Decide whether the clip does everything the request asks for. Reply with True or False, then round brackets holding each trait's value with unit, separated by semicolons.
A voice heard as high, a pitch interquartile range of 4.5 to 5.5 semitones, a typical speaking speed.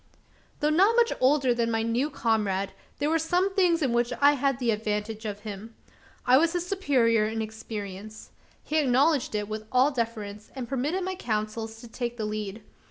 True (235 Hz; 5.2 semitones; 185 wpm)